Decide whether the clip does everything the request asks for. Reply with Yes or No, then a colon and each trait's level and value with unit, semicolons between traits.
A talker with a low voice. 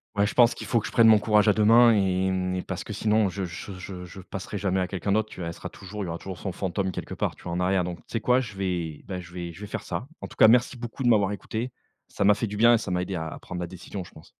Yes: very low, 95 Hz